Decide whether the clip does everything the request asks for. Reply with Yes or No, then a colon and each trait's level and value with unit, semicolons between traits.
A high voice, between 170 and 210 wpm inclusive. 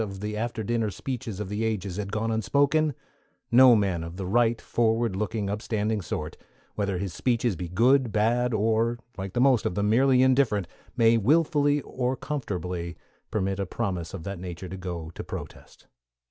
No: low, 110 Hz; average, 175 wpm